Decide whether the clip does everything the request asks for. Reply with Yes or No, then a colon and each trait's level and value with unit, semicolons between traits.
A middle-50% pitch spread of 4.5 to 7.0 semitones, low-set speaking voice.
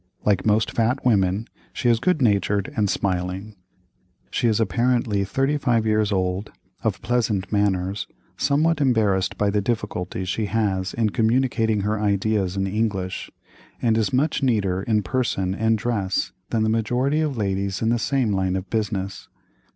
No: average, 3.3 semitones; low, 105 Hz